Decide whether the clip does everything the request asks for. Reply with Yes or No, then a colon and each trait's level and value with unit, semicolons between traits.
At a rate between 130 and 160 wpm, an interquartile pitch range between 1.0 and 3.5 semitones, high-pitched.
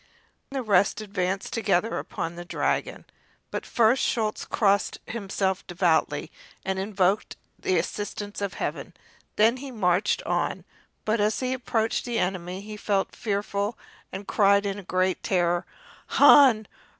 Yes: average, 140 wpm; average, 2.7 semitones; high, 200 Hz